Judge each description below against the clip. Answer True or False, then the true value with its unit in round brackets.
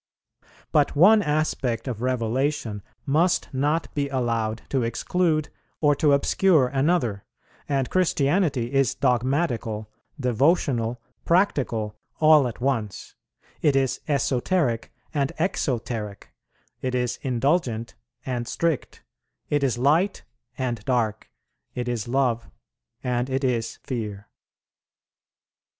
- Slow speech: True (105 wpm)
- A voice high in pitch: False (130 Hz)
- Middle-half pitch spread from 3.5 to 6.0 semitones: True (4.0 semitones)